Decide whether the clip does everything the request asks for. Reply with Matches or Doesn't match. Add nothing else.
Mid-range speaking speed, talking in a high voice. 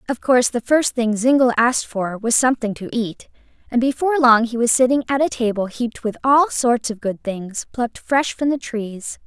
Doesn't match